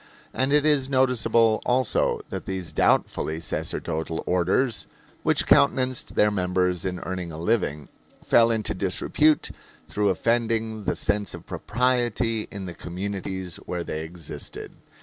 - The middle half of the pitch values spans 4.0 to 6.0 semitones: Yes, average, 5.0 semitones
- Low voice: Yes, low, 100 Hz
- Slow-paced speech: Yes, slow, 130 wpm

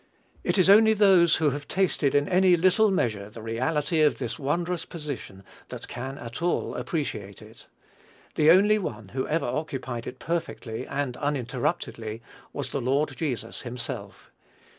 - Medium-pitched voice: Yes, medium, 145 Hz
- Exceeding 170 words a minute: No, average, 155 wpm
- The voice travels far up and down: Yes, wide, 6.0 semitones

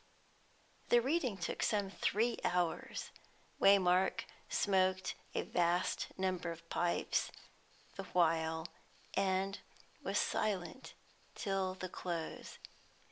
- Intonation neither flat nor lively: No, narrow, 2.1 semitones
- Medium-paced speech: No, slow, 100 wpm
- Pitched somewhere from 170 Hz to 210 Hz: Yes, medium, 185 Hz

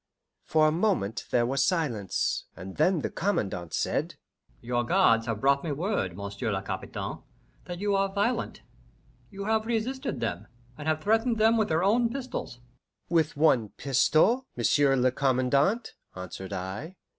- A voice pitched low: No, medium, 155 Hz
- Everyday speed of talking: Yes, average, 155 wpm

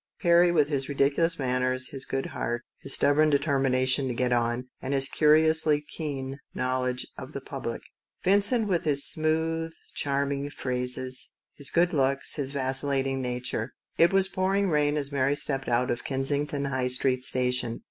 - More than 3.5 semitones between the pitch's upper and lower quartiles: No, average, 3.1 semitones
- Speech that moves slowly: No, average, 160 wpm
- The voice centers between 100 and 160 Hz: Yes, medium, 140 Hz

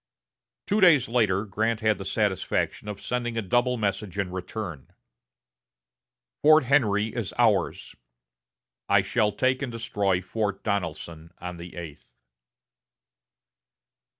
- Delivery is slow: Yes, slow, 120 wpm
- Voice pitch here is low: Yes, low, 105 Hz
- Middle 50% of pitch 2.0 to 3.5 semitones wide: No, average, 4.3 semitones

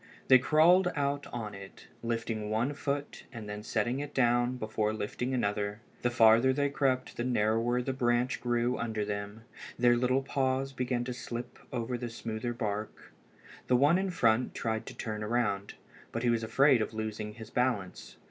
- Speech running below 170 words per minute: No, average, 175 wpm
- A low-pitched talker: Yes, low, 120 Hz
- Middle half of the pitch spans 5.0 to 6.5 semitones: No, average, 2.9 semitones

